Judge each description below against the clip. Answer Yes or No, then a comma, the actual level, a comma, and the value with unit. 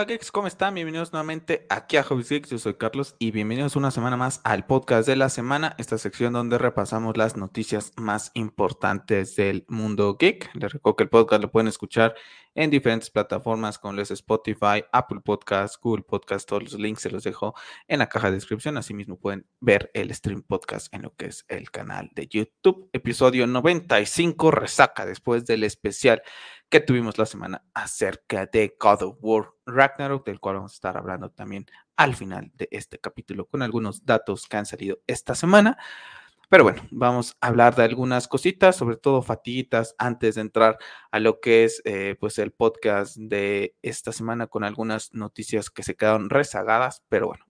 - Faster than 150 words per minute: Yes, average, 185 wpm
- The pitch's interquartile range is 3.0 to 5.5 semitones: Yes, average, 3.5 semitones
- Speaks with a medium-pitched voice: No, low, 115 Hz